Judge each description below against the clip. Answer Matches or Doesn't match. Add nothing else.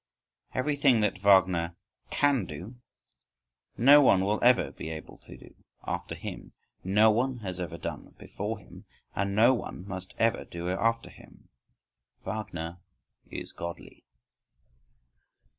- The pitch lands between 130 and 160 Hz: Doesn't match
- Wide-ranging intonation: Doesn't match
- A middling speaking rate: Doesn't match